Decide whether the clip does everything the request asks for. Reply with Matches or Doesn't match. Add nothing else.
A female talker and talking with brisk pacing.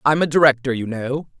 Matches